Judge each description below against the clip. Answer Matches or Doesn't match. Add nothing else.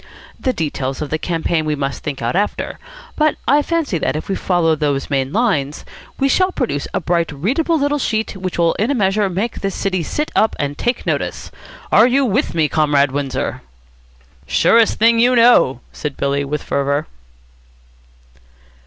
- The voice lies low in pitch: Doesn't match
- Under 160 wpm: Doesn't match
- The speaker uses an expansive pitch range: Matches